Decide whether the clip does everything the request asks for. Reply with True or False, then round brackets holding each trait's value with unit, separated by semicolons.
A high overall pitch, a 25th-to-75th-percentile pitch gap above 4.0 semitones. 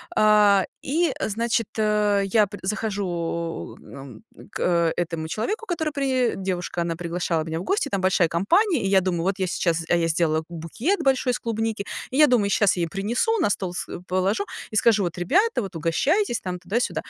True (200 Hz; 5.3 semitones)